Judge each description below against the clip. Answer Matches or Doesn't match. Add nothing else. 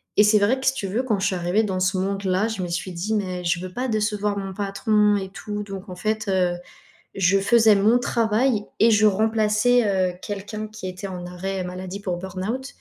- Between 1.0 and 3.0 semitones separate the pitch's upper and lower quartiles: Matches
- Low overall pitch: Doesn't match